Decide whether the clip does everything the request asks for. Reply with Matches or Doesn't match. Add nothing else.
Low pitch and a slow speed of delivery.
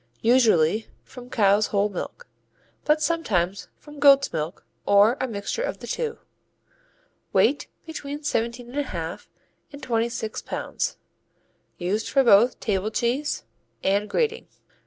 Doesn't match